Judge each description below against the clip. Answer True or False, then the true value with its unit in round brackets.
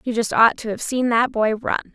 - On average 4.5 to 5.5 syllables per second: True (5.3 syllables/s)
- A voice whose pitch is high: True (230 Hz)